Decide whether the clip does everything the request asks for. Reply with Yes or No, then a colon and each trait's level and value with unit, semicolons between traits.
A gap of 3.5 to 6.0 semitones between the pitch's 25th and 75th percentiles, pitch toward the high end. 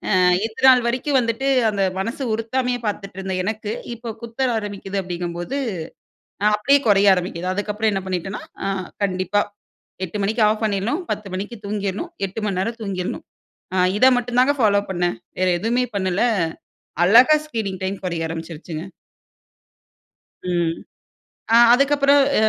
Yes: average, 3.9 semitones; high, 205 Hz